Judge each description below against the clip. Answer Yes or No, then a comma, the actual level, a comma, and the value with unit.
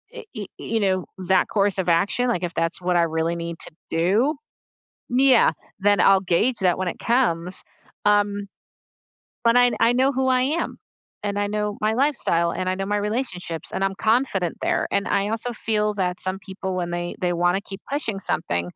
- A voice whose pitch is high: Yes, high, 200 Hz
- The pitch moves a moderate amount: Yes, average, 4.0 semitones